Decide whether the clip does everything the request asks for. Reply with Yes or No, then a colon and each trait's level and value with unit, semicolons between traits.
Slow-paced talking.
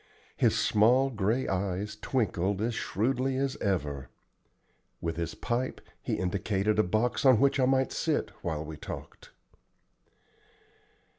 Yes: slow, 130 wpm